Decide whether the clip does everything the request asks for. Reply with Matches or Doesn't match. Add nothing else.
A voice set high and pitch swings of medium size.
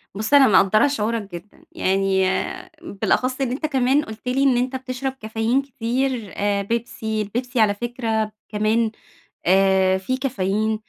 Matches